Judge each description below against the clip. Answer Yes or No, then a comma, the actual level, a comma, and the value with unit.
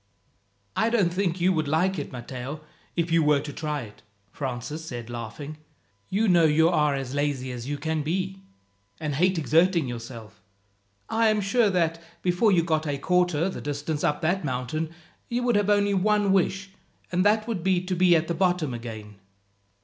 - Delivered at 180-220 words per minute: Yes, average, 185 wpm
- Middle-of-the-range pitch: Yes, medium, 160 Hz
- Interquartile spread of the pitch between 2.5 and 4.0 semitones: No, average, 4.7 semitones